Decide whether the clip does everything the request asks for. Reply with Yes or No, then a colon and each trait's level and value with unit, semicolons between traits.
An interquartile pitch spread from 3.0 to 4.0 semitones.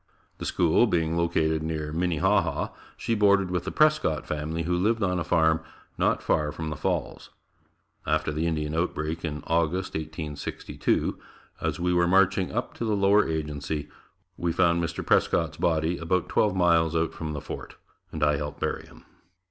No: narrow, 2.6 semitones